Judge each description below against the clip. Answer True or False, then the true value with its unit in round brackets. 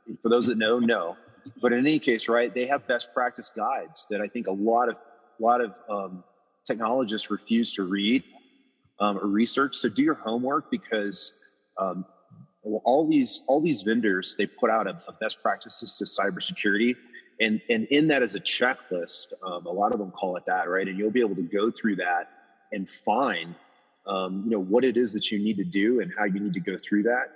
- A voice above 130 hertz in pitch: False (110 Hz)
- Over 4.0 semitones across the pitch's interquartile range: False (3.3 semitones)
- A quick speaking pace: True (215 wpm)